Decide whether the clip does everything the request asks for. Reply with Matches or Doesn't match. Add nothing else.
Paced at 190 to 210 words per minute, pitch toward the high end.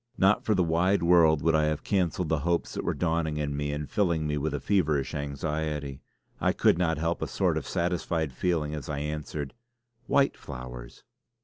Doesn't match